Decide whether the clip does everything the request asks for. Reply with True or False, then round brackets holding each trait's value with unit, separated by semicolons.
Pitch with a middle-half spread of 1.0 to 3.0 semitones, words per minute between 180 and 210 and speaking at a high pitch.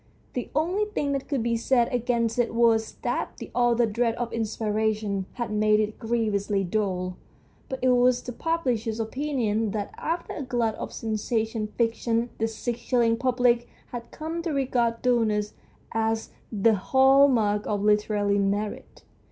False (2.6 semitones; 155 wpm; 230 Hz)